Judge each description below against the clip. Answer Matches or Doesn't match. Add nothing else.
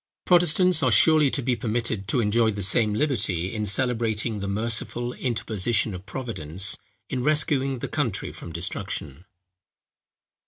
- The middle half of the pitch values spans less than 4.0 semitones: Doesn't match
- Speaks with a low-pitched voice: Matches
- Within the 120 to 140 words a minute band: Matches